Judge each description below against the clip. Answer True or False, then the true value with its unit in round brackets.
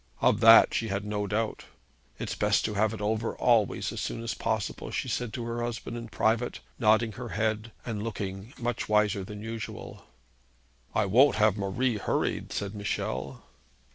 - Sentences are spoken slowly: False (170 wpm)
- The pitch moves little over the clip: True (1.9 semitones)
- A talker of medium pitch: False (110 Hz)